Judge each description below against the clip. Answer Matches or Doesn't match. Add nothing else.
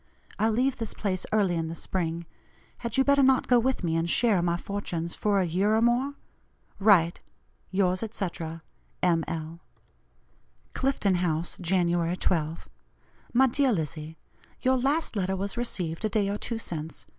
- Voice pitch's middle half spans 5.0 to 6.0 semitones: Matches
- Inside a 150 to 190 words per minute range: Matches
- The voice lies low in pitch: Doesn't match